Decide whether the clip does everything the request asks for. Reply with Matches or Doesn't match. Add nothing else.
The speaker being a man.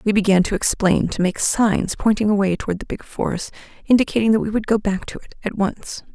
Doesn't match